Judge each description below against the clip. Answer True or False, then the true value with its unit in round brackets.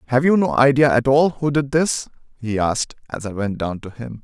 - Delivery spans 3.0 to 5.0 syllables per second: False (5.4 syllables/s)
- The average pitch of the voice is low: True (130 Hz)